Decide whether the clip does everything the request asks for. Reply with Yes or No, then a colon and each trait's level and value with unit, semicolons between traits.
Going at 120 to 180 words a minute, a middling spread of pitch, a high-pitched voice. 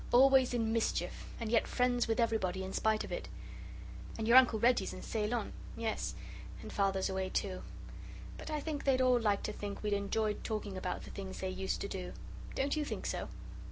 No: average, 195 wpm; average, 3.8 semitones; high, 220 Hz